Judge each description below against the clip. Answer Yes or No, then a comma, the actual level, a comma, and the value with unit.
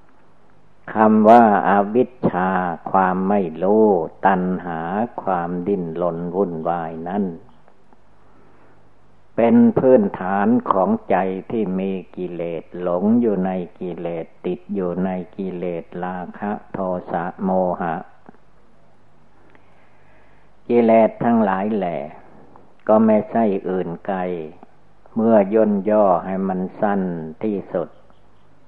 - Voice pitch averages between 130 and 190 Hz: No, very low, 95 Hz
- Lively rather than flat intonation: No, average, 3.4 semitones